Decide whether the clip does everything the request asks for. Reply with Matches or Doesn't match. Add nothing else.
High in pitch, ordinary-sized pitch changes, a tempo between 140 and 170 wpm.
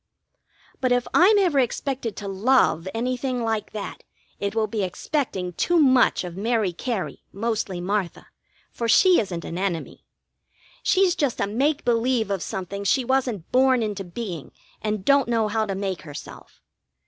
Matches